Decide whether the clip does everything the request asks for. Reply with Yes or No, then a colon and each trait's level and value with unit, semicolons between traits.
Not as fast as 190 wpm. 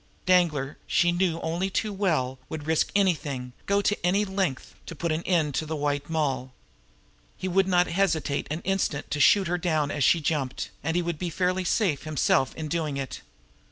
No: average, 195 wpm